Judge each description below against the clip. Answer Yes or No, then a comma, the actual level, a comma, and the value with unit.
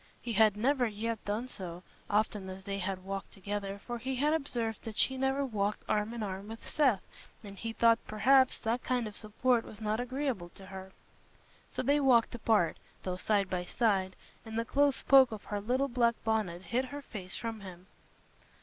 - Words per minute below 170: No, average, 195 wpm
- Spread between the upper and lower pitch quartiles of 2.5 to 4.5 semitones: Yes, average, 3.9 semitones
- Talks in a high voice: Yes, high, 220 Hz